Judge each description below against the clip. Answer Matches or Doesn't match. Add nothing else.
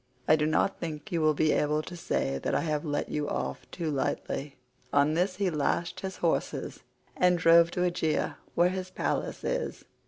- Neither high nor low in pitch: Matches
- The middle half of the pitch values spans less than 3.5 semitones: Matches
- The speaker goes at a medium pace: Matches